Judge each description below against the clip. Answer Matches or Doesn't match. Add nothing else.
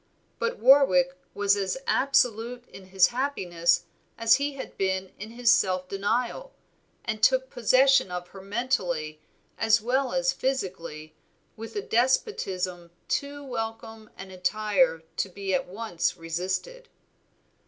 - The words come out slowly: Matches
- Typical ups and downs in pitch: Doesn't match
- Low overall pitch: Doesn't match